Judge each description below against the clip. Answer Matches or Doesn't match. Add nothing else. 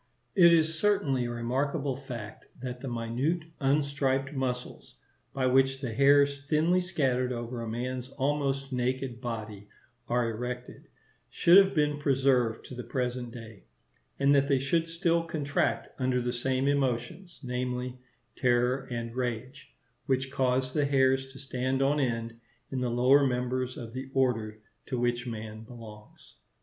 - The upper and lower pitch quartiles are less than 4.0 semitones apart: Matches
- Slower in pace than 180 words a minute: Matches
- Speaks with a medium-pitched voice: Doesn't match